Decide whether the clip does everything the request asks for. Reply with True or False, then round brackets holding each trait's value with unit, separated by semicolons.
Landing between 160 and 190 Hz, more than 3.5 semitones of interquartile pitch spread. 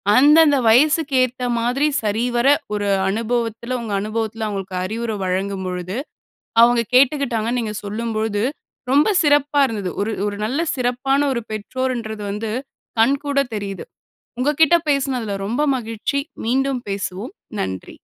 False (230 Hz; 4.1 semitones)